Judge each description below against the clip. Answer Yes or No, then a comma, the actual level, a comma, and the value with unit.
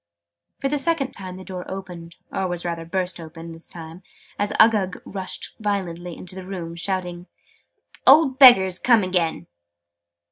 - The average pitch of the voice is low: No, medium, 185 Hz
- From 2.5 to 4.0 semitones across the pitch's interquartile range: Yes, average, 2.8 semitones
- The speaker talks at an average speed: Yes, average, 155 wpm